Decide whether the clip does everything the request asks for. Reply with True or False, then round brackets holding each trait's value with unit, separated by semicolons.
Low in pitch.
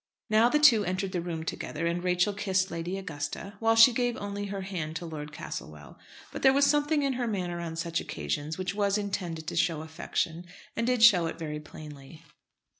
False (180 Hz)